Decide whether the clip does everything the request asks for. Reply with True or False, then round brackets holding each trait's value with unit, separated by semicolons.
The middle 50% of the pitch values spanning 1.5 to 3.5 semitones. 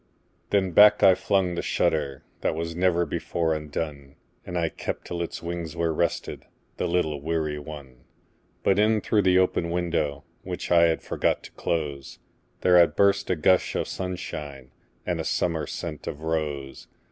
True (2.9 semitones)